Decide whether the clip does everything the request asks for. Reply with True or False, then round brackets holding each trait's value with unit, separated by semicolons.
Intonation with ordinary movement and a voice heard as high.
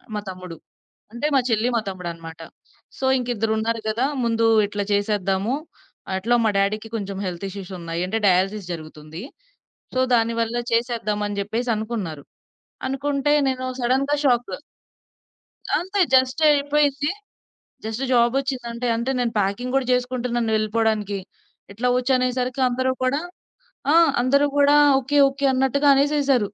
True (4.2 semitones; 235 Hz)